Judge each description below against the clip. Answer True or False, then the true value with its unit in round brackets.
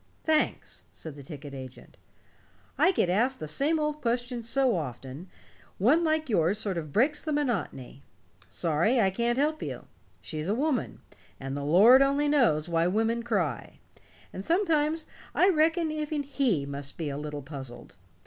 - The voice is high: True (225 Hz)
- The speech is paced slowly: False (160 wpm)